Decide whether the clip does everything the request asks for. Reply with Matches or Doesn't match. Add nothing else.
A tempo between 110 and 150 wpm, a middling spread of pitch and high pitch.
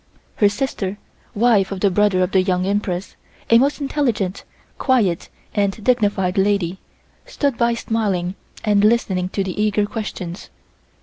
Matches